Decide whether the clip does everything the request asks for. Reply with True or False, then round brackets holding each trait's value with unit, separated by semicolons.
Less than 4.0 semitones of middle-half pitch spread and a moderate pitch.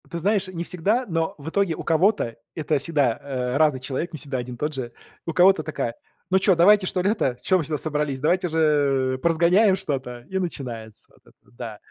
False (5.6 semitones; 155 Hz)